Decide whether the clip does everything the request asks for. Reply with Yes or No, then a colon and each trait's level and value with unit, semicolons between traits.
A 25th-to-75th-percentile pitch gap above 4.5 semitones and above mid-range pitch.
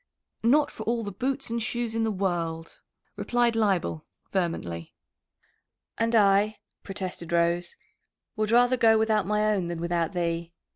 Yes: average, 4.9 semitones; high, 205 Hz